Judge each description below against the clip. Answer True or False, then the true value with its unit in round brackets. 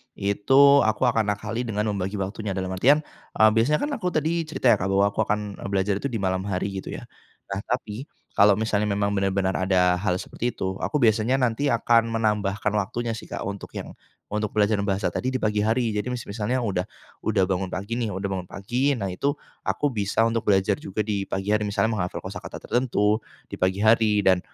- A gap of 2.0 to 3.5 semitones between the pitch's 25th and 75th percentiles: True (2.8 semitones)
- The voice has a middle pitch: False (105 Hz)